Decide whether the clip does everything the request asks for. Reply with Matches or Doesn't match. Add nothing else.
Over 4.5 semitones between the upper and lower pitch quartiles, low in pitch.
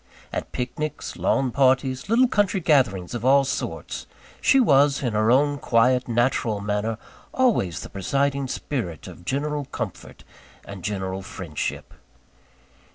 Matches